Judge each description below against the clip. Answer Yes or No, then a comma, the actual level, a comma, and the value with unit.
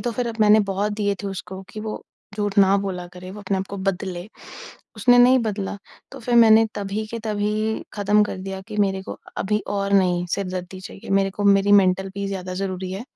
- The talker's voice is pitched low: No, high, 200 Hz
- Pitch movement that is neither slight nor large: No, narrow, 1.8 semitones